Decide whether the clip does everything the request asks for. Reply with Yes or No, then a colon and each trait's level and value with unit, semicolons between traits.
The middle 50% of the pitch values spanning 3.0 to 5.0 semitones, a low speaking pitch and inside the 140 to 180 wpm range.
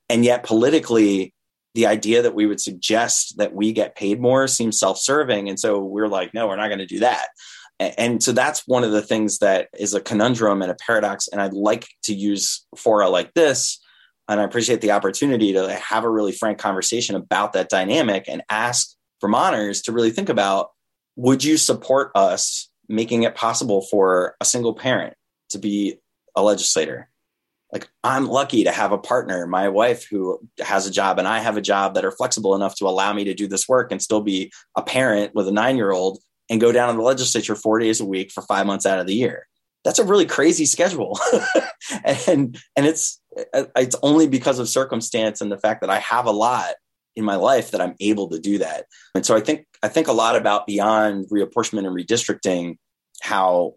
No: average, 3.4 semitones; low, 110 Hz; fast, 205 wpm